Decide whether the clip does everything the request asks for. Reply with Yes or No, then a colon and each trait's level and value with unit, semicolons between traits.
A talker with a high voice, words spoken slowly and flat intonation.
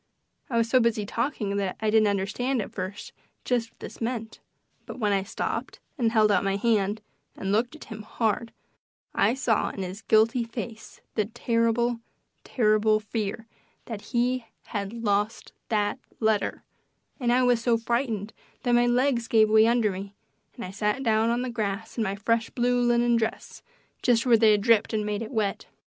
No: high, 225 Hz; average, 185 wpm; narrow, 2.3 semitones